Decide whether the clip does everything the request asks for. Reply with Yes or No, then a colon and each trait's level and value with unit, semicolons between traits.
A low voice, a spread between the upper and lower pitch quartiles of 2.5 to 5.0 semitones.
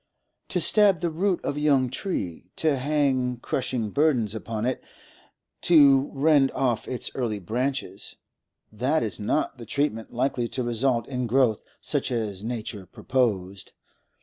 Yes: low, 125 Hz; average, 4.2 semitones